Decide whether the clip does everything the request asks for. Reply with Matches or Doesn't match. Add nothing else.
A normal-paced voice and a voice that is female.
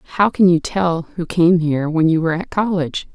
Doesn't match